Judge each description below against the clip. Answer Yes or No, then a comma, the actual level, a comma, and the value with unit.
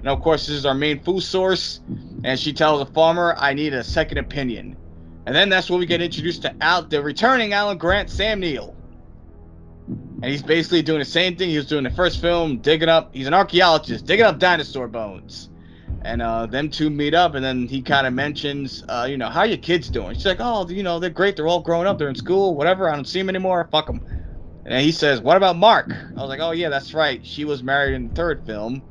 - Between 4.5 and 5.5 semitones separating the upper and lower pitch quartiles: Yes, average, 5.1 semitones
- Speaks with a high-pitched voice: No, medium, 150 Hz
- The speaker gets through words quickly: Yes, fast, 250 wpm